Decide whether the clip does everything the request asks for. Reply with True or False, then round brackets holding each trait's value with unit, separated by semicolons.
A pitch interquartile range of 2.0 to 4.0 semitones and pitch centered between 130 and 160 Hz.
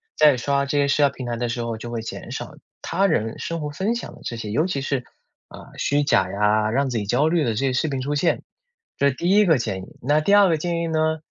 False (5.1 semitones; 140 Hz)